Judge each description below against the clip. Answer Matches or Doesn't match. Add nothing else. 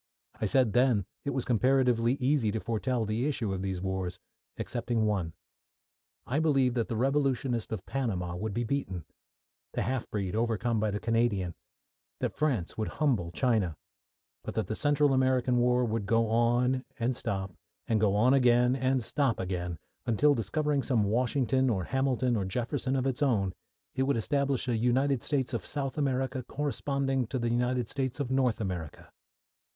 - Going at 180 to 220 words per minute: Doesn't match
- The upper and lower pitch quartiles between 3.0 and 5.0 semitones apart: Matches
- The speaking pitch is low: Matches